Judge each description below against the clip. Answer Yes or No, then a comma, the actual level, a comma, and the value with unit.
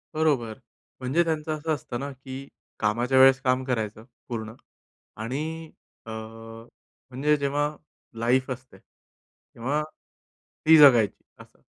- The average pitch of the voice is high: No, low, 130 Hz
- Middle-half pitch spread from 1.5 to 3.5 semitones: No, average, 4.1 semitones